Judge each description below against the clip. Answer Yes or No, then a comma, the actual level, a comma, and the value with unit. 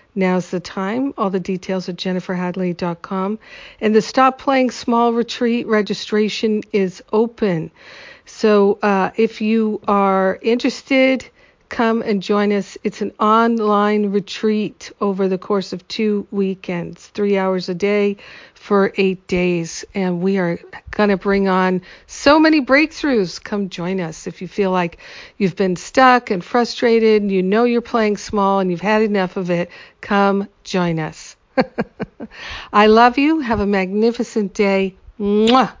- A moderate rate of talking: Yes, average, 150 wpm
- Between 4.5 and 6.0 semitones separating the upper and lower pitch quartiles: No, average, 3.0 semitones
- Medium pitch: No, high, 205 Hz